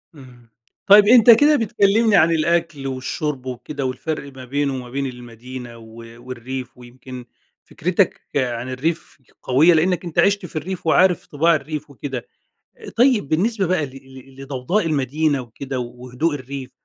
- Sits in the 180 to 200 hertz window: No, medium, 140 Hz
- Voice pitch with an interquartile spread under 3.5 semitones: No, average, 4.9 semitones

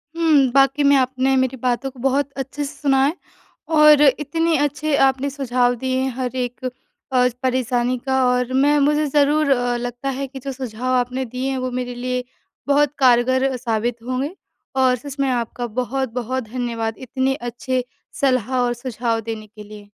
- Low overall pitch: No, very high, 260 Hz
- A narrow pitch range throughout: Yes, narrow, 1.9 semitones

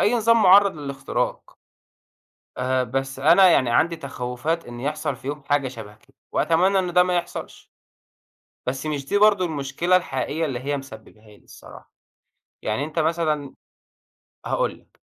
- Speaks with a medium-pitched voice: Yes, medium, 145 Hz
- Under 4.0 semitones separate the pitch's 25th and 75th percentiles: No, average, 4.7 semitones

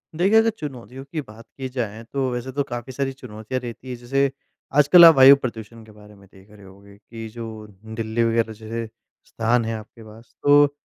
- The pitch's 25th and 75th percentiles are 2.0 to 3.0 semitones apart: No, average, 3.5 semitones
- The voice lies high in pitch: No, low, 115 Hz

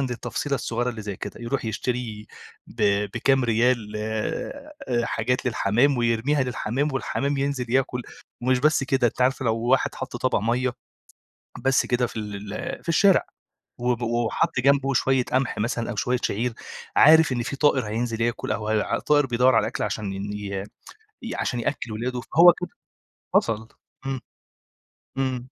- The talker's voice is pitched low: Yes, low, 125 Hz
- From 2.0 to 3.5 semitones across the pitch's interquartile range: Yes, average, 2.9 semitones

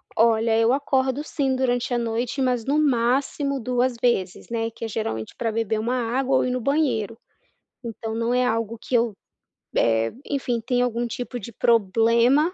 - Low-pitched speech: No, high, 240 Hz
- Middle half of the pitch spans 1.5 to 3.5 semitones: Yes, narrow, 2.4 semitones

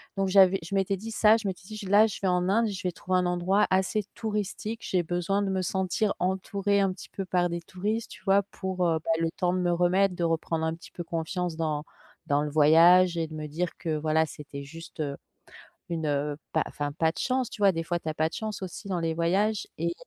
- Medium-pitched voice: Yes, medium, 180 Hz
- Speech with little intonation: No, average, 3.1 semitones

